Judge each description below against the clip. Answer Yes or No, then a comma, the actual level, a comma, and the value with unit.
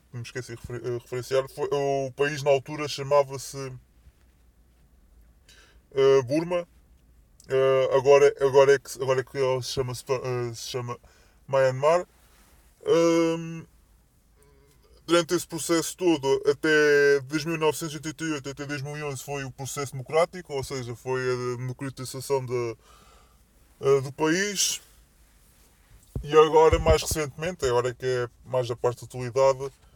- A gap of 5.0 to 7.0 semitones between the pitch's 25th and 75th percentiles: No, average, 3.3 semitones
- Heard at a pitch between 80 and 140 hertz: Yes, low, 135 Hz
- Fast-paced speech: No, average, 130 wpm